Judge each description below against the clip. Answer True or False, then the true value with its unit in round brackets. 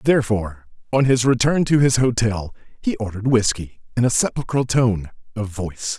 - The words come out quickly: False (160 wpm)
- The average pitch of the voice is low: True (115 Hz)